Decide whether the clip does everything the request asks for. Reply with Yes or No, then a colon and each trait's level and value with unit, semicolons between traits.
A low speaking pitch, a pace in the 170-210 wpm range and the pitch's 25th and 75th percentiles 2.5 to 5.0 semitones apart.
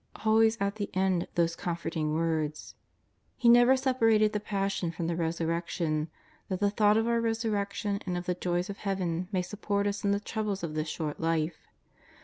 No: high, 190 Hz; average, 185 wpm; average, 4.0 semitones